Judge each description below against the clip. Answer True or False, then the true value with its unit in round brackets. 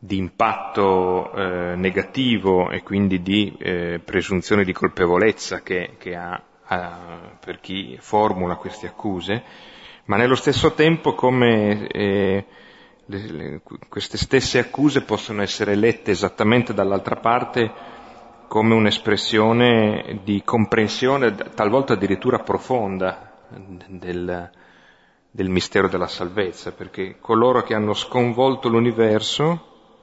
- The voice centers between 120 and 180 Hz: False (105 Hz)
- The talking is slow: True (110 wpm)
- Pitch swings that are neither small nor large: True (3.7 semitones)